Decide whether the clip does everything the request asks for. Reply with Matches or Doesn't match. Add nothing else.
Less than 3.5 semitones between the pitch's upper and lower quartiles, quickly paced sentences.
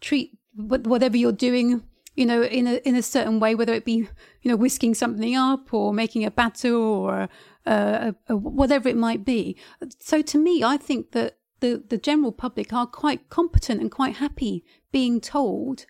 Doesn't match